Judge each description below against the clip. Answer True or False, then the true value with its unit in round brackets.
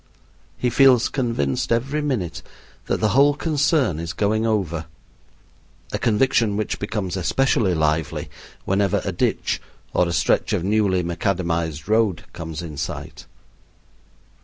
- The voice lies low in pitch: True (100 Hz)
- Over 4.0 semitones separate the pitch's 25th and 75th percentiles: True (5.6 semitones)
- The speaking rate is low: True (130 wpm)